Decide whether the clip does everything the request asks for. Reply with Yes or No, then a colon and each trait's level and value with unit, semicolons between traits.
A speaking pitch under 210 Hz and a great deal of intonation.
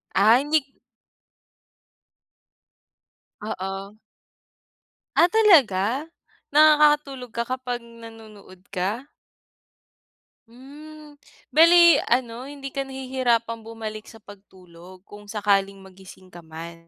No: high, 230 Hz; wide, 5.7 semitones